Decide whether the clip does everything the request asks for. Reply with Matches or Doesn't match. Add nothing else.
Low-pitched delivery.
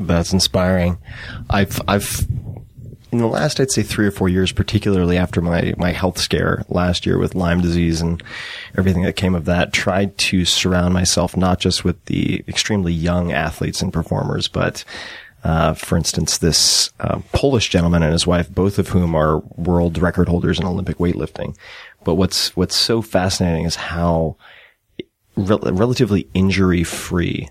Matches